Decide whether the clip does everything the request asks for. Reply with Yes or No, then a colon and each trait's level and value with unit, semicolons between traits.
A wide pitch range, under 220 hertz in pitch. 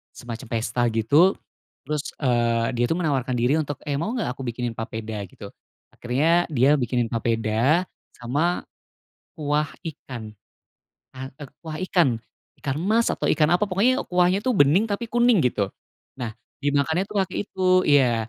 Yes: wide, 6.5 semitones; medium, 140 Hz